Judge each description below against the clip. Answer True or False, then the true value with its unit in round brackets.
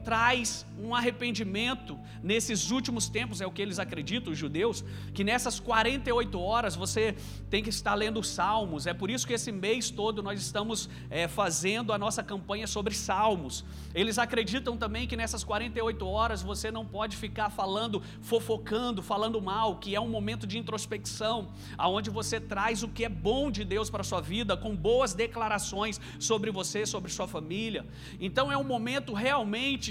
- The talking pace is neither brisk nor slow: True (170 wpm)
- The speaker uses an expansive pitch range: False (2.7 semitones)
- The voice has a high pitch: True (215 Hz)